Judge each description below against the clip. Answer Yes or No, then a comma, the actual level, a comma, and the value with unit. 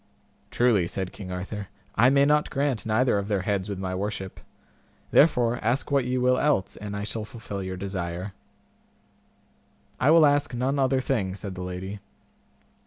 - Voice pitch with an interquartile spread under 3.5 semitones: No, average, 5.1 semitones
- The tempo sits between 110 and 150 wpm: No, average, 170 wpm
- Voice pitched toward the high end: No, low, 105 Hz